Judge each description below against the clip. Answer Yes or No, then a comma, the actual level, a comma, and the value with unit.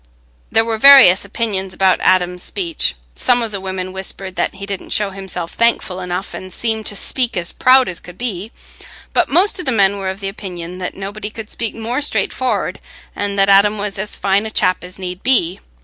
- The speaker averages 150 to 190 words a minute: No, fast, 205 wpm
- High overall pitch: Yes, high, 200 Hz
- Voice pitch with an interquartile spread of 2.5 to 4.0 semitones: Yes, average, 3.2 semitones